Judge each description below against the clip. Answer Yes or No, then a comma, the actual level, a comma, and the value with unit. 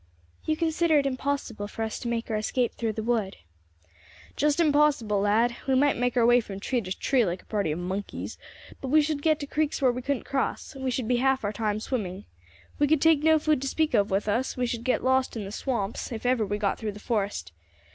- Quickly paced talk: Yes, fast, 235 wpm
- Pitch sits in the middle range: No, high, 245 Hz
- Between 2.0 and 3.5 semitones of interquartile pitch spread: No, average, 4.9 semitones